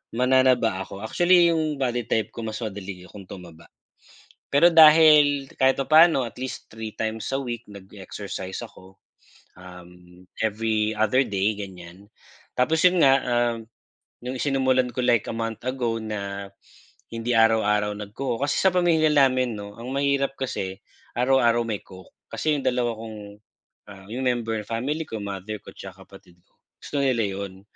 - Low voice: Yes, low, 115 Hz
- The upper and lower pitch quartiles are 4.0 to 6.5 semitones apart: Yes, average, 4.8 semitones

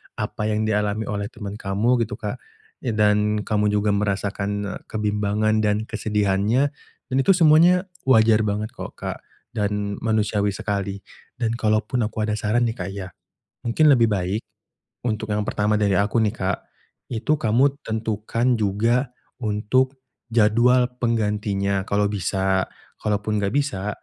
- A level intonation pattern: Yes, narrow, 2.2 semitones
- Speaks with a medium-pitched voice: No, low, 105 Hz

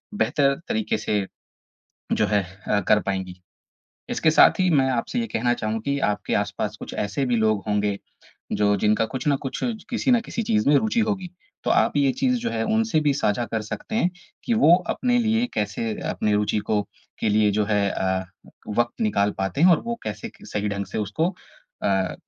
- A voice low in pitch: Yes, low, 115 Hz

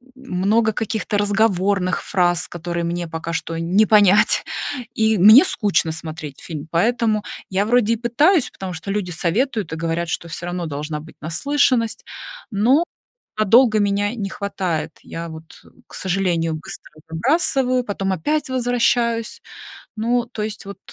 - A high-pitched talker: Yes, high, 200 Hz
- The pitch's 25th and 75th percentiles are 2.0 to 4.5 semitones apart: No, average, 5.2 semitones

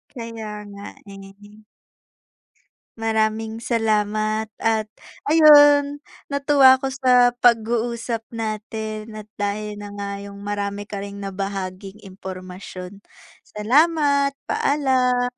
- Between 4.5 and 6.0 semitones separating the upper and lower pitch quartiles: No, average, 3.4 semitones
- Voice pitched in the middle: No, high, 215 Hz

